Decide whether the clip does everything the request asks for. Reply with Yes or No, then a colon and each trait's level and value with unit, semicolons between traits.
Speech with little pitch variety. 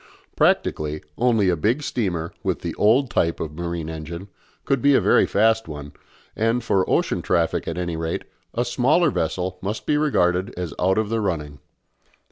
No: wide, 5.6 semitones